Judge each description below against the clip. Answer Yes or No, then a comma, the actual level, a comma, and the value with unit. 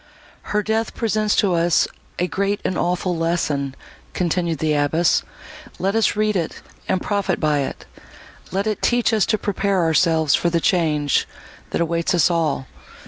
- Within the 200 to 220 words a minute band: No, average, 160 wpm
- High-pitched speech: No, medium, 175 Hz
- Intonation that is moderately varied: Yes, average, 3.8 semitones